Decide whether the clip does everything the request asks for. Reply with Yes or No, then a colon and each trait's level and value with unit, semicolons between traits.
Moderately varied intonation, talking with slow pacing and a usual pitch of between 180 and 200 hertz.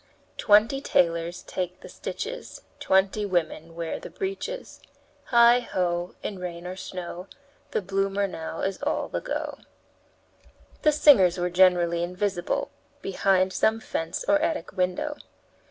Yes: average, 4.0 semitones; slow, 130 wpm; medium, 185 Hz